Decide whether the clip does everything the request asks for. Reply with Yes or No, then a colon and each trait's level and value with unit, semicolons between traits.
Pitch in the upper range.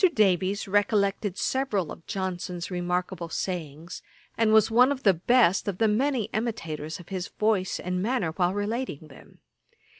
Yes: high, 195 Hz